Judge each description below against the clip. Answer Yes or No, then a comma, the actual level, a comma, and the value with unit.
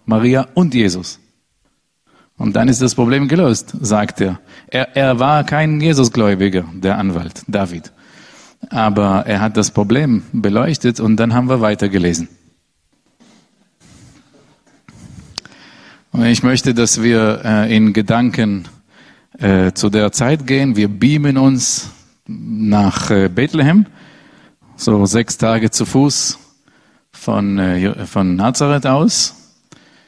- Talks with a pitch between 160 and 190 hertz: No, low, 110 Hz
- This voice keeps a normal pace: No, slow, 120 wpm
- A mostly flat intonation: No, average, 4.5 semitones